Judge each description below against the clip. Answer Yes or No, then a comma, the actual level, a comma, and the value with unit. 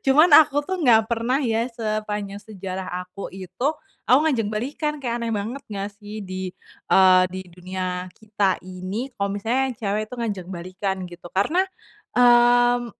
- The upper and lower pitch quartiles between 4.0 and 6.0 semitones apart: Yes, average, 4.3 semitones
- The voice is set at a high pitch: Yes, high, 215 Hz